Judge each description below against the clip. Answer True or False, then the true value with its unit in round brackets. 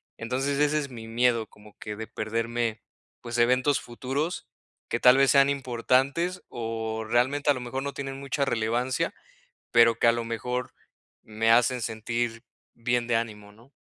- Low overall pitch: True (120 Hz)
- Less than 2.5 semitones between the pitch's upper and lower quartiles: False (2.8 semitones)